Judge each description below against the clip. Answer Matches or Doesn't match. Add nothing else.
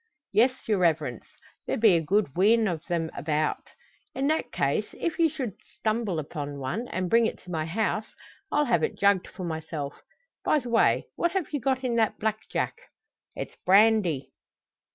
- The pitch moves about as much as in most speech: Doesn't match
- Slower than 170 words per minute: Doesn't match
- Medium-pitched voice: Doesn't match